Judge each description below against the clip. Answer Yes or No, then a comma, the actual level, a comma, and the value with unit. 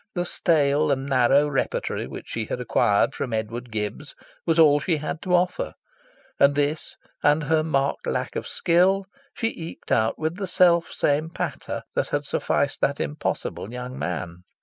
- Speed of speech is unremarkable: Yes, average, 170 wpm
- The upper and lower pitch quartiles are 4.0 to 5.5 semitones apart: Yes, average, 5.0 semitones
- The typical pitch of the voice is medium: Yes, medium, 145 Hz